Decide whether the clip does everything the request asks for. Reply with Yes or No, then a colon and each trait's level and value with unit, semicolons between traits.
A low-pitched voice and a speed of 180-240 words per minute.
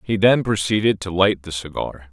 Yes: very low, 95 Hz; average, 200 wpm